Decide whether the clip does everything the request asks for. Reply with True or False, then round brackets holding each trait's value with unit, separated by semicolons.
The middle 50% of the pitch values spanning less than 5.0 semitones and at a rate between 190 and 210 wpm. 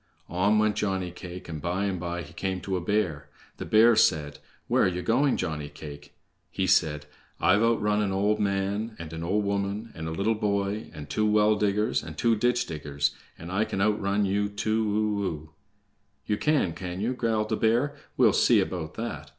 True (3.8 semitones; 200 wpm)